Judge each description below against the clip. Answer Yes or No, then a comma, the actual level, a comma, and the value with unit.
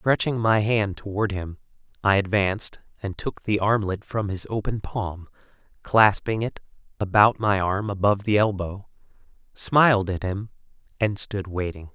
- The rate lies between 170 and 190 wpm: No, average, 145 wpm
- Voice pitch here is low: Yes, low, 100 Hz